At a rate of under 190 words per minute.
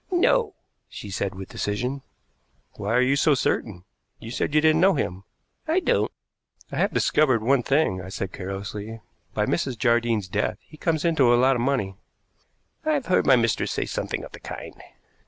Yes: average, 180 wpm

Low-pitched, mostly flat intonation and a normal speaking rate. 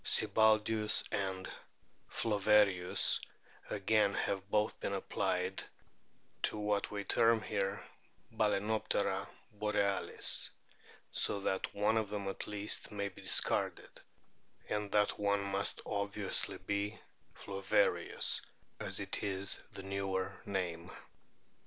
No: low, 100 Hz; narrow, 1.4 semitones; slow, 105 wpm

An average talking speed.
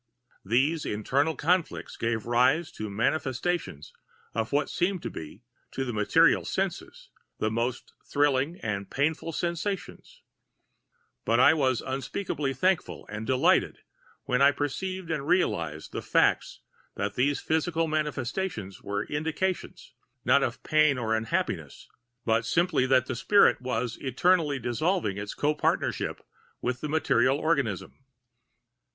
No: slow, 130 wpm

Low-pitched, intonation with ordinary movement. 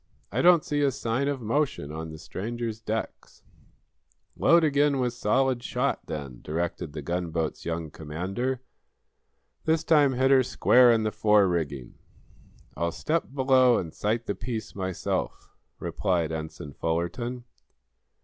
No: low, 110 Hz; wide, 7.9 semitones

